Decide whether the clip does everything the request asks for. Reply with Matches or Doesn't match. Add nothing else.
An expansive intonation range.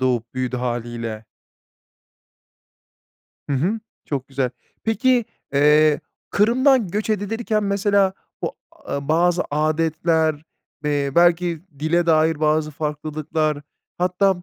Doesn't match